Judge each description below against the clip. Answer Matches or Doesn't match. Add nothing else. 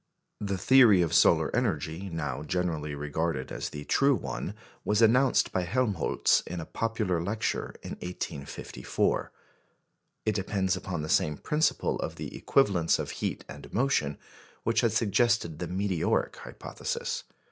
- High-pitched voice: Doesn't match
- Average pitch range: Doesn't match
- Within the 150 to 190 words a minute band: Doesn't match